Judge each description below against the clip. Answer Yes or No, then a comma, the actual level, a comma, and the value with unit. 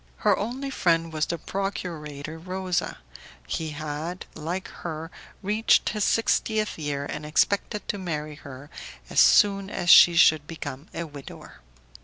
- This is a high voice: No, medium, 165 Hz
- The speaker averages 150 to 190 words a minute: No, average, 140 wpm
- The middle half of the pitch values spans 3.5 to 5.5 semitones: Yes, average, 4.4 semitones